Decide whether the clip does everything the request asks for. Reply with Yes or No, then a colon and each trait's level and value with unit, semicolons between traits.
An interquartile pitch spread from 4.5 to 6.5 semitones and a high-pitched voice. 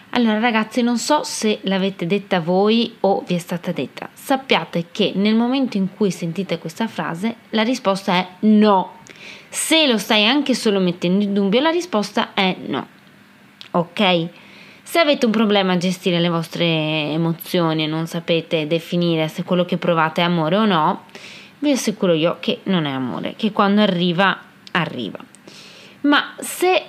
No: average, 4.1 semitones; high, 195 Hz